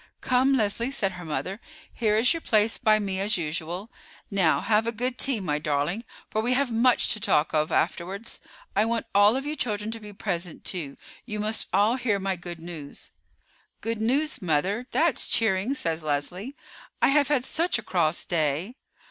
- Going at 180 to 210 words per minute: Yes, average, 185 wpm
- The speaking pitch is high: Yes, high, 210 Hz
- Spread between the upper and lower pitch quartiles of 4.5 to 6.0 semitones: Yes, wide, 5.4 semitones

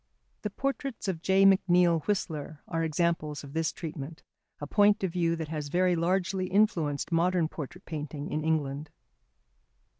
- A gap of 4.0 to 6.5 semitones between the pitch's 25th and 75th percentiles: No, average, 3.3 semitones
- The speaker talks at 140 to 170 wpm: Yes, average, 150 wpm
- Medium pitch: Yes, medium, 165 Hz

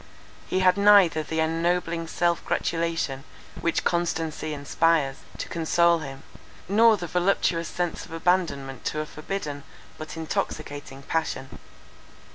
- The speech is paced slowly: Yes, slow, 120 wpm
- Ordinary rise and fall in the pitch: No, narrow, 2.3 semitones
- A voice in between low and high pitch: Yes, medium, 165 Hz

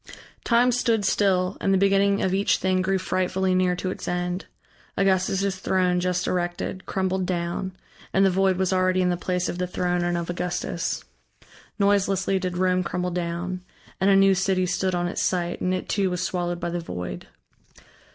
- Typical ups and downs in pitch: No, narrow, 1.3 semitones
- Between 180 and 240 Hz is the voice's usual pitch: Yes, medium, 185 Hz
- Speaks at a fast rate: No, average, 185 wpm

